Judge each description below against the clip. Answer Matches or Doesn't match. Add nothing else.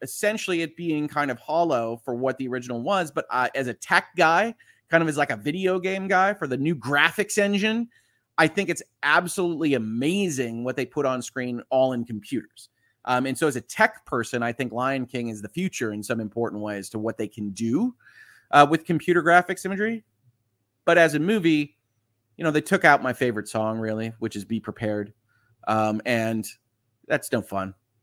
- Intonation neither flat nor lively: Doesn't match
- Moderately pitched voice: Doesn't match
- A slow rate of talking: Doesn't match